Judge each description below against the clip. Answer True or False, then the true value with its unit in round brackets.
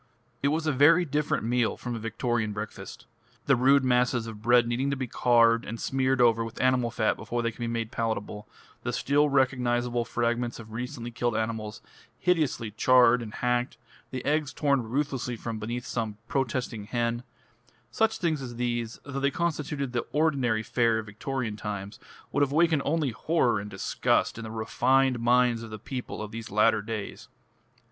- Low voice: True (120 Hz)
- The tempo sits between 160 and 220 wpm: True (180 wpm)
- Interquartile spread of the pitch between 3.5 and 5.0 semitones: False (2.9 semitones)